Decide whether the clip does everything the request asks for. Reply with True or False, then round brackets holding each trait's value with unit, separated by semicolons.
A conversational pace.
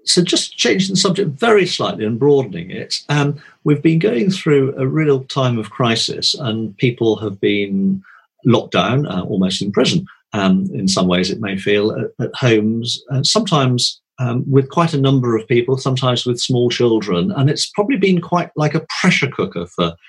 True (190 wpm)